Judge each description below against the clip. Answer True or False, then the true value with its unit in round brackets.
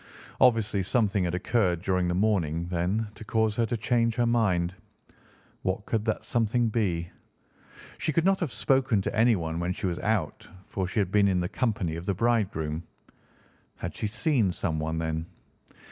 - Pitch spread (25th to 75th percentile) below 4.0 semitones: False (4.6 semitones)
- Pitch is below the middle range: True (100 Hz)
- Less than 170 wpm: False (175 wpm)